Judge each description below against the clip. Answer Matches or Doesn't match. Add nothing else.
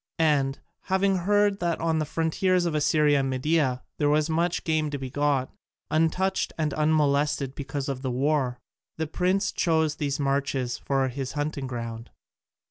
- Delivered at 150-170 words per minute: Matches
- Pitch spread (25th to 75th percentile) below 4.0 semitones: Matches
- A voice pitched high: Doesn't match